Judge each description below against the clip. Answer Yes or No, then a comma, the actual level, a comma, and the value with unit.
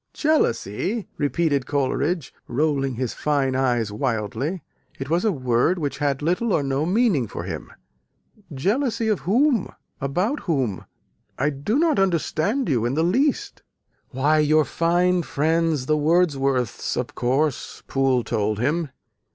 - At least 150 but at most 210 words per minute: No, slow, 135 wpm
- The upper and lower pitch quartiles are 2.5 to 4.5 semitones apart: No, wide, 5.5 semitones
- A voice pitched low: No, medium, 150 Hz